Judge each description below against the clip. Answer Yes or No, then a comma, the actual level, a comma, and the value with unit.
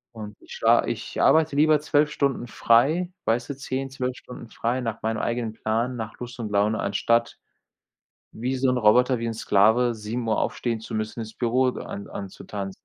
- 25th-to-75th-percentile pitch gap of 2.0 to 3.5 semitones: Yes, average, 2.7 semitones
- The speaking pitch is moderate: No, low, 120 Hz